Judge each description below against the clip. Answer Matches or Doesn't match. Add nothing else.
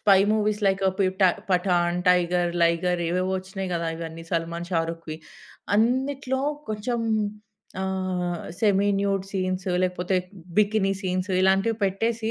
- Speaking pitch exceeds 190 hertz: Doesn't match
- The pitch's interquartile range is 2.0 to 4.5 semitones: Matches